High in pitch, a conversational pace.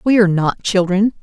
Yes: high, 195 Hz; average, 195 wpm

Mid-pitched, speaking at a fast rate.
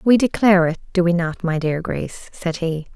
Yes: medium, 180 Hz; fast, 225 wpm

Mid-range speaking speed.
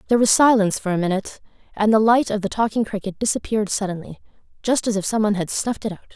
No: fast, 225 wpm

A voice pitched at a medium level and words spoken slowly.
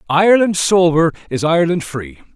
Yes: medium, 165 Hz; slow, 125 wpm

